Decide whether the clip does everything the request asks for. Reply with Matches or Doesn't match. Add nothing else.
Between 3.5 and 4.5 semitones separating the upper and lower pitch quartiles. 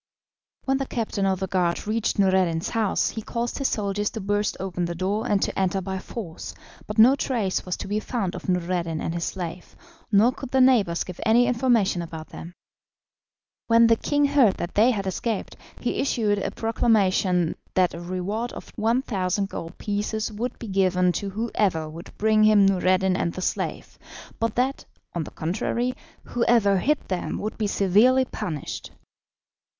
Matches